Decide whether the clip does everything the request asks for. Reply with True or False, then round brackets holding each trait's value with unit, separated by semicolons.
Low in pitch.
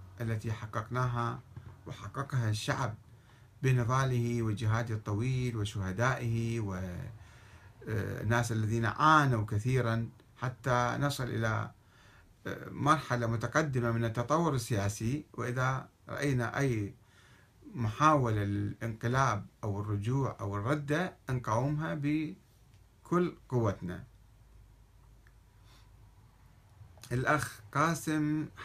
True (120 Hz)